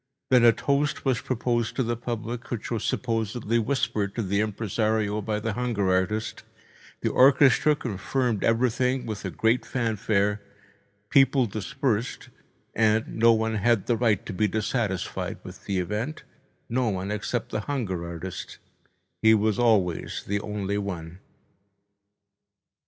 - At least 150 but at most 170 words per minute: No, slow, 135 wpm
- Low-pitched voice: Yes, low, 110 Hz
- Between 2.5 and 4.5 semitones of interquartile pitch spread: Yes, average, 2.9 semitones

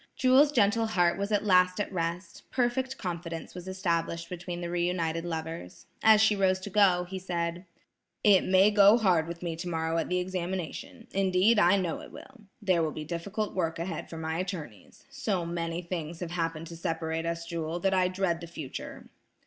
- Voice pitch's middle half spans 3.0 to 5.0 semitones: No, narrow, 2.6 semitones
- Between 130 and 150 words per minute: No, average, 190 wpm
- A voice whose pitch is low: No, medium, 180 Hz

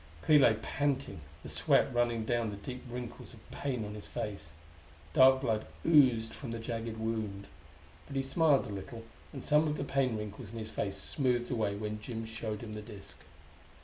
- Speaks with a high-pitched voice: No, low, 115 Hz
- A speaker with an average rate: Yes, average, 190 wpm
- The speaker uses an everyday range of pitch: Yes, average, 3.5 semitones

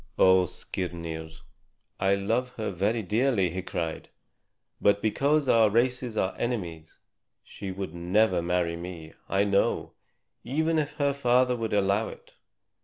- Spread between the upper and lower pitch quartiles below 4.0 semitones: No, average, 5.2 semitones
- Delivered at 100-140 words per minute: Yes, slow, 135 wpm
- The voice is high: No, low, 100 Hz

